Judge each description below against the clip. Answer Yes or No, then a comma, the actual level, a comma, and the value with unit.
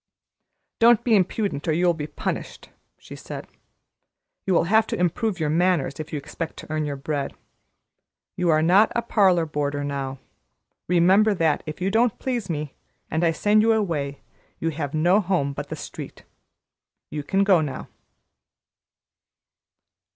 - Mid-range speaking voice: Yes, medium, 170 Hz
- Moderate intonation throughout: Yes, average, 4.8 semitones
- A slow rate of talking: No, average, 160 wpm